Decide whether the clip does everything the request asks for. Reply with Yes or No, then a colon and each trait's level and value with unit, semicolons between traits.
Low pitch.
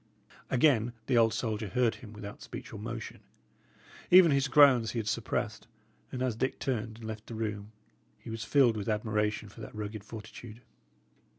Yes: low, 115 Hz